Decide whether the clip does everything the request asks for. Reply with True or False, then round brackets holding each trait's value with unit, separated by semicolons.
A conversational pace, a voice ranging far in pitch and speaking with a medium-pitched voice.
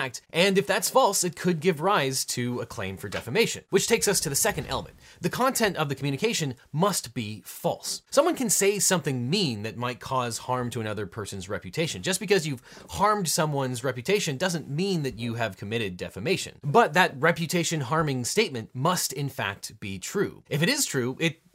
True (190 wpm; 7.3 semitones; 155 Hz)